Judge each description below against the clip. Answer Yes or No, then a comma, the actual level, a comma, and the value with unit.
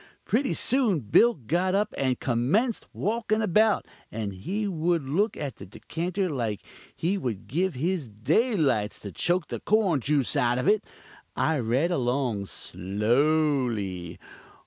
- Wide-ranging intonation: Yes, wide, 8.7 semitones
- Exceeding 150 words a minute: No, average, 140 wpm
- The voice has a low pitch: No, medium, 150 Hz